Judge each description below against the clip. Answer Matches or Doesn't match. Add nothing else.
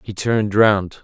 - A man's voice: Matches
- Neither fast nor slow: Matches